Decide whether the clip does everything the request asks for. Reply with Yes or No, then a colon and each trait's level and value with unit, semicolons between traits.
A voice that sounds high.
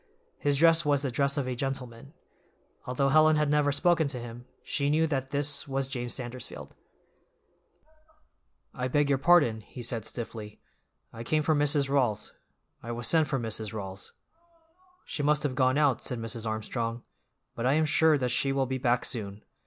No: low, 135 Hz